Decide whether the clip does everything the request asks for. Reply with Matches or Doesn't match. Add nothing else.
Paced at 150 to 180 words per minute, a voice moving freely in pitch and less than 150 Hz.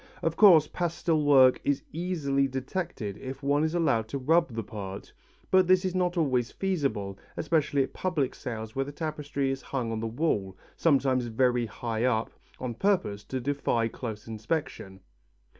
Matches